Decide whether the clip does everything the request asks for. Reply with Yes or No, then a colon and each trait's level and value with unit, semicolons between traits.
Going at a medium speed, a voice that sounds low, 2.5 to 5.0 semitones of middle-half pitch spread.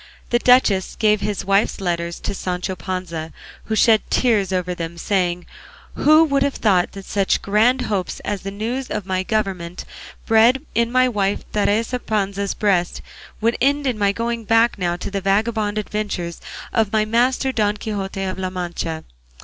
No: average, 170 wpm; high, 205 Hz; average, 3.5 semitones